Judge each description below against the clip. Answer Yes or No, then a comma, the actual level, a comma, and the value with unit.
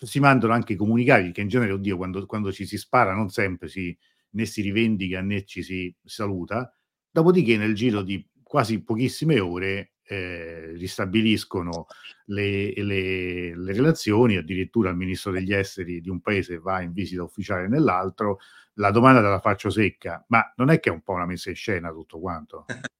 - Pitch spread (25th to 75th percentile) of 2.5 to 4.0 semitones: Yes, average, 3.3 semitones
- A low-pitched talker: Yes, low, 100 Hz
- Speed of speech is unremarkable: No, fast, 175 wpm